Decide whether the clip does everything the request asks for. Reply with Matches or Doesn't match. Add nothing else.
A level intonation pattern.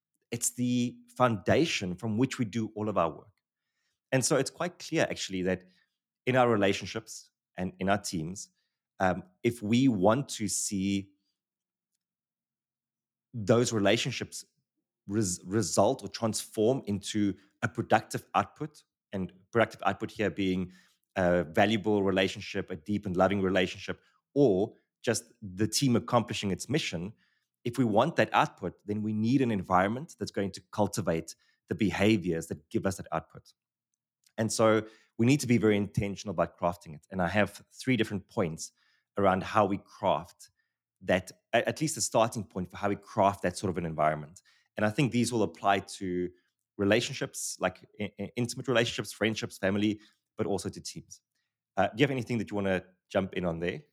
Doesn't match